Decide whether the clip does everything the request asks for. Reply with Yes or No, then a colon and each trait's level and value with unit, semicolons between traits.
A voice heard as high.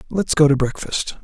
No: medium, 150 Hz